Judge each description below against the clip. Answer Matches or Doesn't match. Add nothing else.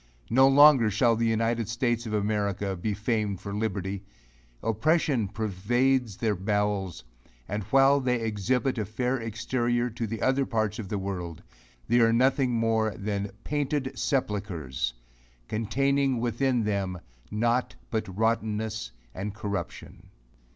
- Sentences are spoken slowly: Matches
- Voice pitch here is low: Matches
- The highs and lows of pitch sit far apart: Doesn't match